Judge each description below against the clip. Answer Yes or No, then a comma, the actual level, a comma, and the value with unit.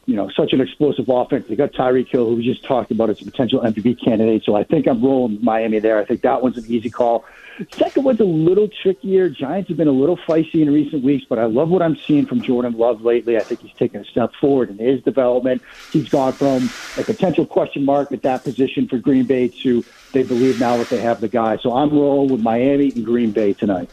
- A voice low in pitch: Yes, low, 130 Hz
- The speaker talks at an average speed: No, fast, 250 wpm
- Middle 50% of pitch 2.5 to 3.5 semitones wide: Yes, average, 3.0 semitones